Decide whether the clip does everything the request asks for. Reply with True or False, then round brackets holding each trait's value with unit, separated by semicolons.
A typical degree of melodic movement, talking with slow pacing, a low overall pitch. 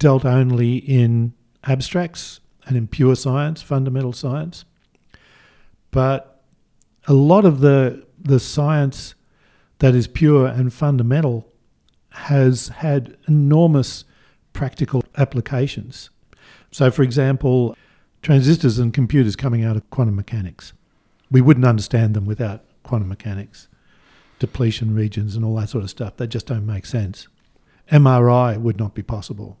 True (3.5 semitones; 130 wpm; 125 Hz)